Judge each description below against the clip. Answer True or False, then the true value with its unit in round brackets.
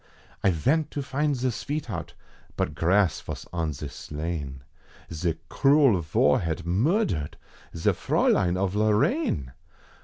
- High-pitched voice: False (90 Hz)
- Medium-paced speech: False (125 wpm)